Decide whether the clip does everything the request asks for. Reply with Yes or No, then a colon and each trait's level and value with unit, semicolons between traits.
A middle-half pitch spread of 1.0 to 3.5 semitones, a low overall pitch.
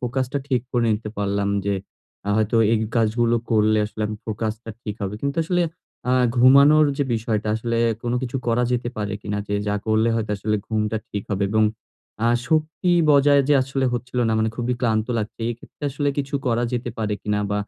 Yes: average, 3.2 semitones; low, 115 Hz